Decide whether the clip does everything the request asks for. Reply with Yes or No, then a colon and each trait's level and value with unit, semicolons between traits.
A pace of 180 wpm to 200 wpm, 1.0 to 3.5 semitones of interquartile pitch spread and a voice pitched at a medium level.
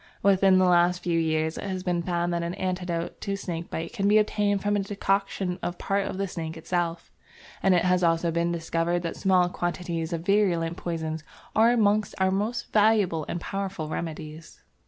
Yes: average, 190 wpm; average, 2.8 semitones; medium, 180 Hz